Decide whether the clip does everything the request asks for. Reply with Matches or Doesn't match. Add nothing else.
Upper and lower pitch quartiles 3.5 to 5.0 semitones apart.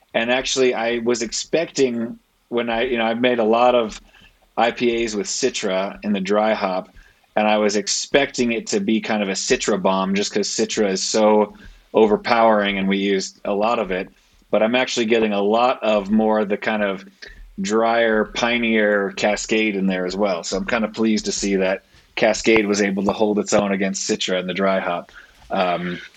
Doesn't match